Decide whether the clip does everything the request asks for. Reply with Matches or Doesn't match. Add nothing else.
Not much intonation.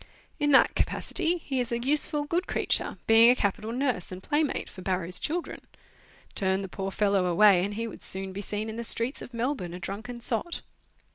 Doesn't match